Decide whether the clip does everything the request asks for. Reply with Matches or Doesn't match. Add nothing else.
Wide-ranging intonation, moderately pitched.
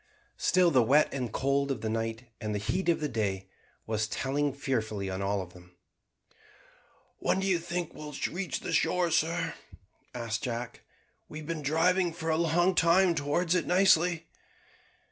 Matches